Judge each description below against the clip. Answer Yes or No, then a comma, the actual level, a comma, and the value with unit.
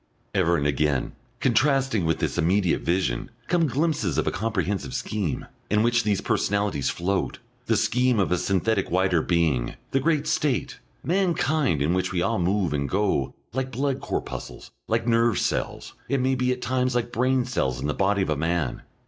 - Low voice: Yes, low, 105 Hz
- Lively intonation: Yes, wide, 6.6 semitones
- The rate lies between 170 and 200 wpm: Yes, average, 180 wpm